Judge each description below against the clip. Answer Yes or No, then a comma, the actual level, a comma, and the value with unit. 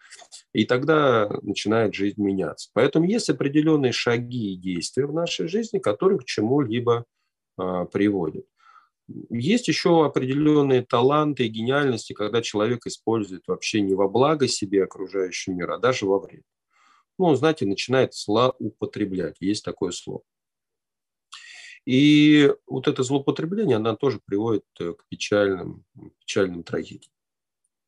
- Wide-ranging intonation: Yes, wide, 6.9 semitones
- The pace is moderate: Yes, average, 125 wpm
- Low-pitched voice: Yes, low, 120 Hz